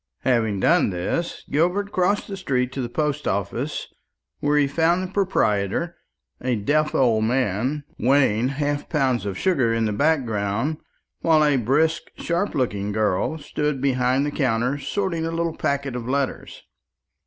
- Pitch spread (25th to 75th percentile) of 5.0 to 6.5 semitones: Yes, wide, 5.5 semitones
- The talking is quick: No, average, 155 wpm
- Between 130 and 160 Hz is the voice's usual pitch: Yes, medium, 140 Hz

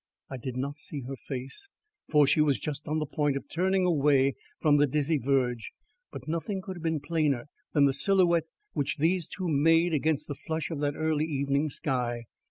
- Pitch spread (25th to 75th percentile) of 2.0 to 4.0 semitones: Yes, average, 2.8 semitones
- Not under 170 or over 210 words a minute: Yes, average, 195 wpm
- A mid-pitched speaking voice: Yes, medium, 150 Hz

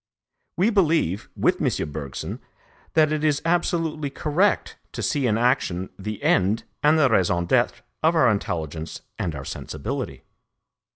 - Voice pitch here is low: Yes, low, 125 Hz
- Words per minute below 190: Yes, average, 140 wpm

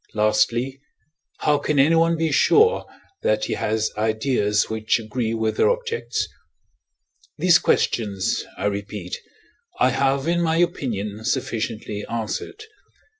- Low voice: Yes, low, 115 Hz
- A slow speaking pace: Yes, slow, 120 wpm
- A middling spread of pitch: No, wide, 6.9 semitones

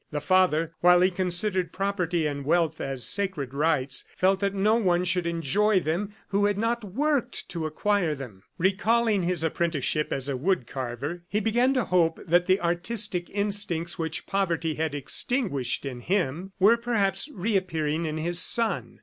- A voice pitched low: No, medium, 180 Hz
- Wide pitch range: No, average, 4.2 semitones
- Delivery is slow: No, average, 165 wpm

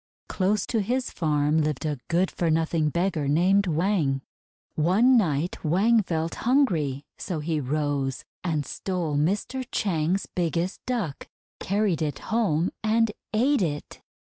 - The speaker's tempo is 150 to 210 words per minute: No, slow, 135 wpm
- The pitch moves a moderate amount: Yes, average, 5.0 semitones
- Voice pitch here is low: No, medium, 170 Hz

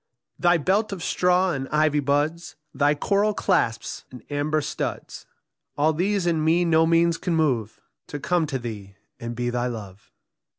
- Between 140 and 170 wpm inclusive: Yes, average, 165 wpm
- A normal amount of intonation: Yes, average, 5.0 semitones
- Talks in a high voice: No, medium, 155 Hz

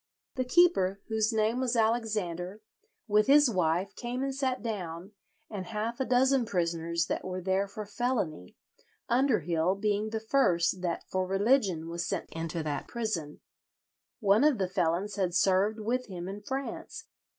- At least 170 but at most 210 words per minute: No, average, 155 wpm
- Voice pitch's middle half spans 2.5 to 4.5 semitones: No, average, 4.9 semitones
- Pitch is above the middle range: Yes, high, 205 Hz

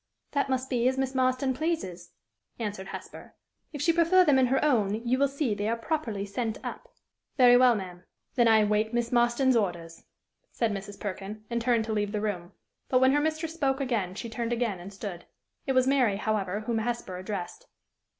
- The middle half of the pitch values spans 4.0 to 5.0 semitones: Yes, average, 4.3 semitones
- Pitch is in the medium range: No, high, 235 Hz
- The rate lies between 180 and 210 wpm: Yes, average, 200 wpm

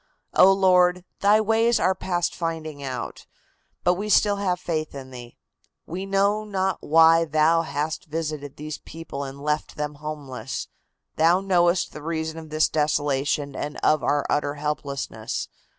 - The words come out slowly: No, average, 150 wpm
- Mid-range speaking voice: Yes, medium, 160 Hz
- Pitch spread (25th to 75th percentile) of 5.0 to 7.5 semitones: No, average, 3.7 semitones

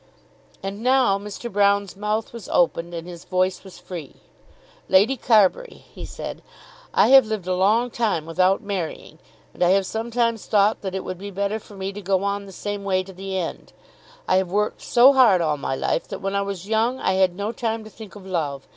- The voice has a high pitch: Yes, high, 200 Hz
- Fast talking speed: Yes, fast, 215 wpm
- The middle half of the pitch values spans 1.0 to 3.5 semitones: Yes, average, 2.7 semitones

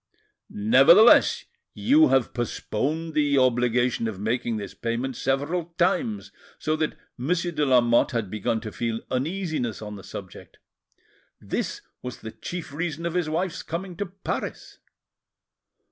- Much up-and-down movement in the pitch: Yes, wide, 6.4 semitones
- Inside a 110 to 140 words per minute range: Yes, slow, 135 wpm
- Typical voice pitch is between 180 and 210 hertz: No, low, 135 Hz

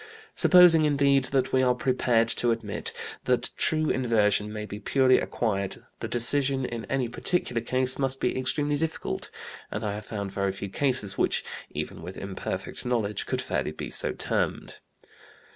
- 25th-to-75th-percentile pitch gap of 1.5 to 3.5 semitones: No, average, 4.2 semitones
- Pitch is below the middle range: Yes, low, 125 Hz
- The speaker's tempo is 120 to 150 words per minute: No, average, 160 wpm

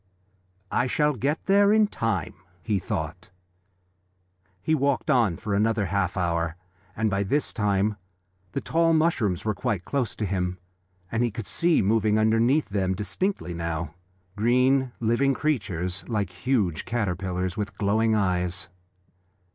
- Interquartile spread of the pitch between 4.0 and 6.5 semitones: Yes, wide, 5.5 semitones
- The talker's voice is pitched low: Yes, low, 105 Hz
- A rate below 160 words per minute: Yes, average, 140 wpm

